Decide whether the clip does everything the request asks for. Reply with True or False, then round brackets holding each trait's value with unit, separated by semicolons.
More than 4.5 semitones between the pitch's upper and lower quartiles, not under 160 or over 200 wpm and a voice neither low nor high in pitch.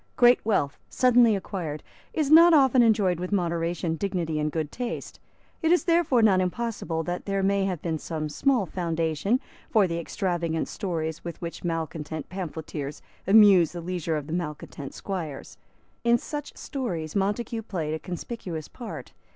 False (5.6 semitones; 150 wpm; 180 Hz)